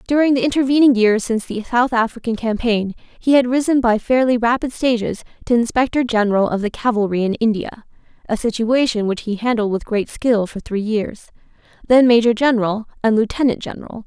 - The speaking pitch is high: Yes, high, 230 Hz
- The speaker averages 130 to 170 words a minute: Yes, average, 165 wpm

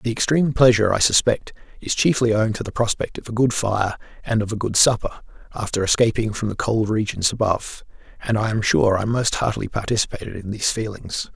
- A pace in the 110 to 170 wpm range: No, average, 200 wpm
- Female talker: No, male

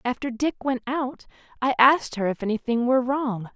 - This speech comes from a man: No, female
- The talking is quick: No, average, 185 wpm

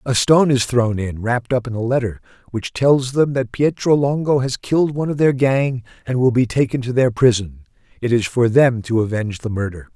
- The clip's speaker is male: Yes, male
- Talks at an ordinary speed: No, fast, 225 wpm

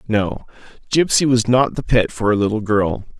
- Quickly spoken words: No, average, 190 wpm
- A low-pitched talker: Yes, low, 115 Hz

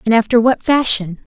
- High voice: Yes, high, 225 Hz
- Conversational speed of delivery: Yes, average, 175 wpm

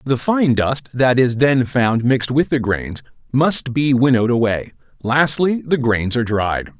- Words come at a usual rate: Yes, average, 175 wpm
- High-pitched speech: No, low, 130 Hz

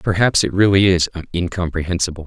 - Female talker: No, male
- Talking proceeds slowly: Yes, slow, 130 wpm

